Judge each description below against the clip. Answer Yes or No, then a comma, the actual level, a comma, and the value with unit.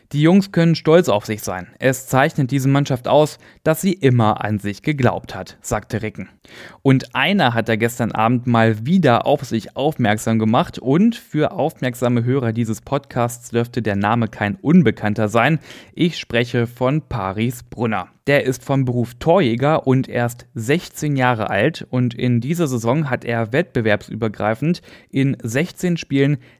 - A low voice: Yes, low, 125 Hz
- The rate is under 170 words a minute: Yes, average, 160 wpm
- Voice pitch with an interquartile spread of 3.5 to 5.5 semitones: Yes, average, 4.0 semitones